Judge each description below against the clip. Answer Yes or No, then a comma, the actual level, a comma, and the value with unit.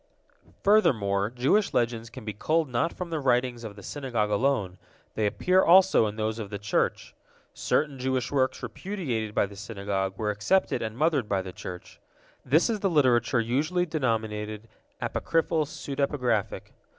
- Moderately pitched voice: No, low, 120 Hz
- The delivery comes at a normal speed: Yes, average, 155 wpm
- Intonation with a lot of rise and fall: Yes, wide, 5.9 semitones